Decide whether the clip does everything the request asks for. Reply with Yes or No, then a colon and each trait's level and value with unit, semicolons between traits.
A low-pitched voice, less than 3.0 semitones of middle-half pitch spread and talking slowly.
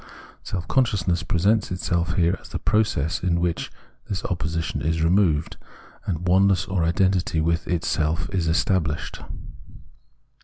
Yes: very low, 85 Hz; narrow, 2.6 semitones; slow, 125 wpm